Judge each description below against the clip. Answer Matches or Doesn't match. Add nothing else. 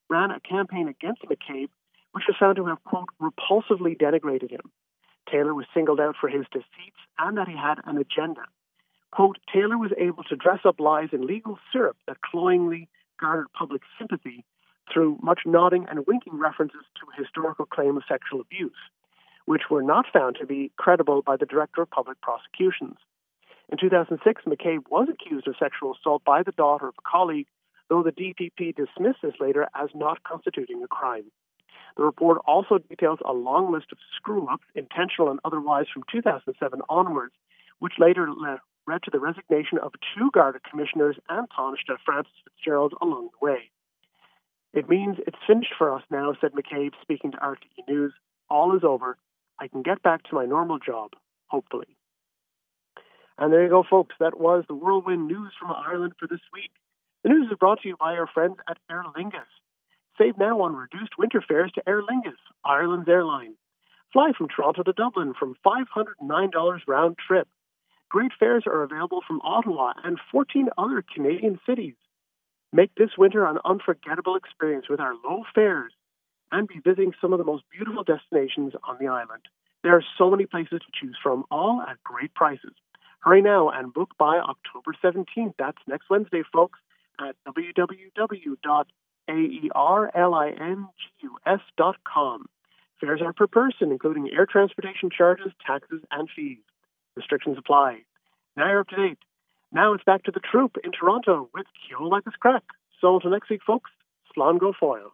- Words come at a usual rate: Matches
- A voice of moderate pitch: Matches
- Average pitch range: Matches